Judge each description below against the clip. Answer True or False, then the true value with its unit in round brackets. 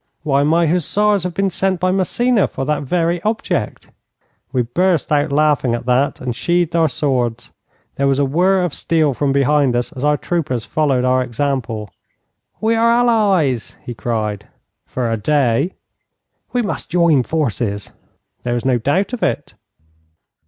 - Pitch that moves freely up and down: True (6.0 semitones)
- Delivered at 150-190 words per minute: True (160 wpm)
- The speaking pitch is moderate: True (145 Hz)